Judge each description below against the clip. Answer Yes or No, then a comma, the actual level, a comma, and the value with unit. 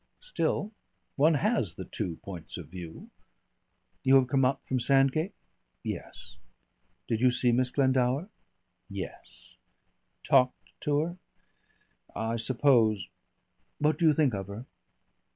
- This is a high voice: No, low, 130 Hz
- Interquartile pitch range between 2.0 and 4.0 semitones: No, average, 4.6 semitones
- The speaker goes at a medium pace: No, slow, 125 wpm